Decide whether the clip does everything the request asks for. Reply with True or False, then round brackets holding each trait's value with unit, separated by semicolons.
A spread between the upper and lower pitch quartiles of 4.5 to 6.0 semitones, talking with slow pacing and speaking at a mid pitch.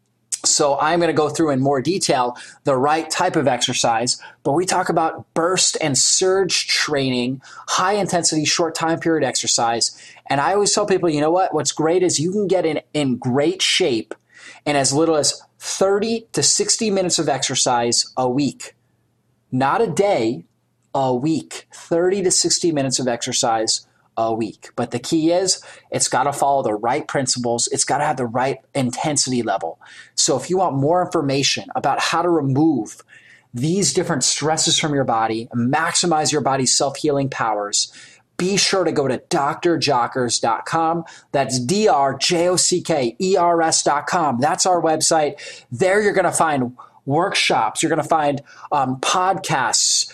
False (5.0 semitones; 170 wpm; 155 Hz)